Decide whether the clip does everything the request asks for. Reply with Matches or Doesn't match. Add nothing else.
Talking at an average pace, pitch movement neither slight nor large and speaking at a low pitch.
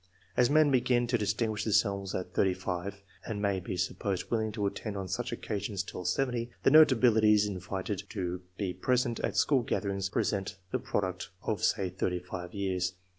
Matches